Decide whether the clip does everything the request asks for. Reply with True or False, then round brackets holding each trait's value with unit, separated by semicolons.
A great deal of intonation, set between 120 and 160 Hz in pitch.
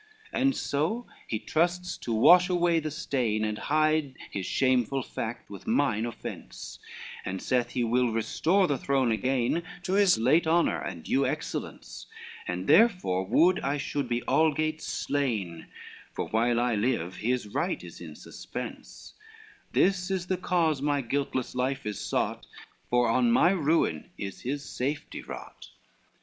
True (5.9 semitones; 135 Hz)